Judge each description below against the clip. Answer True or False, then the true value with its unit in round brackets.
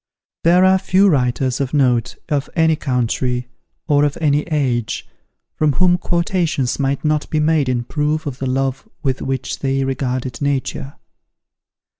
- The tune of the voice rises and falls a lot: False (3.2 semitones)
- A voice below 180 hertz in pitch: True (140 Hz)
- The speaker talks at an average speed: True (150 wpm)